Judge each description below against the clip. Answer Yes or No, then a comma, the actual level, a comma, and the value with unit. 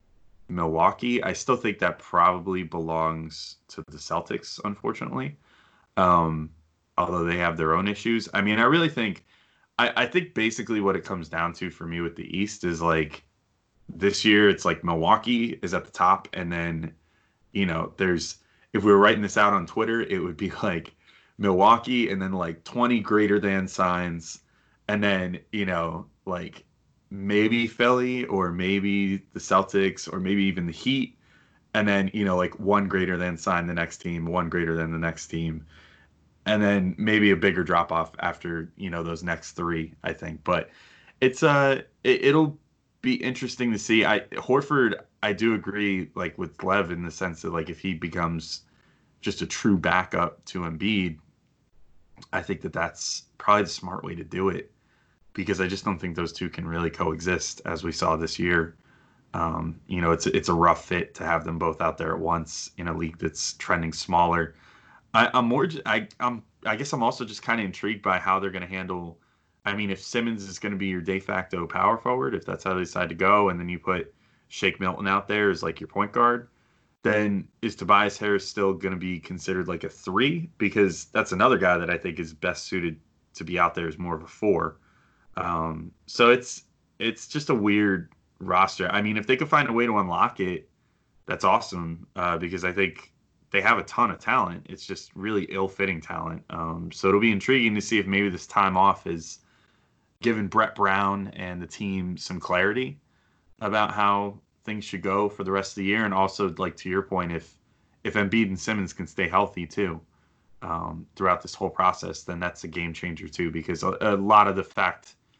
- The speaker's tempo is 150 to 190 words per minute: No, average, 200 wpm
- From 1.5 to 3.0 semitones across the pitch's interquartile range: No, average, 3.8 semitones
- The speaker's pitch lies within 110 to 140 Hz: No, very low, 95 Hz